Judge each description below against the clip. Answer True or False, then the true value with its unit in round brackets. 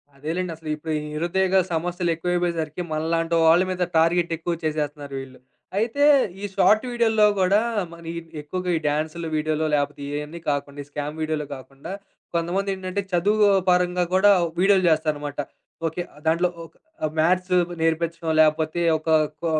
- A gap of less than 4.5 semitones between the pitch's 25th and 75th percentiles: True (2.8 semitones)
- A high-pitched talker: False (165 Hz)